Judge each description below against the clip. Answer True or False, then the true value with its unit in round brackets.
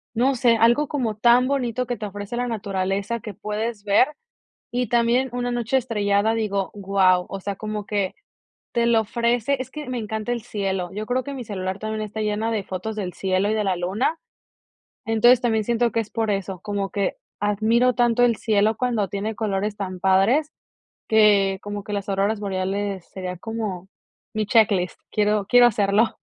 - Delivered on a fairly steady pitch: False (3.0 semitones)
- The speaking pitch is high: True (215 Hz)